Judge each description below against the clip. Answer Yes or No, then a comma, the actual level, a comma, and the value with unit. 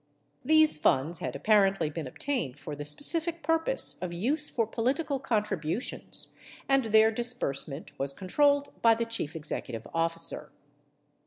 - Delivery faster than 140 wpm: No, slow, 135 wpm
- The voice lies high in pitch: Yes, high, 215 Hz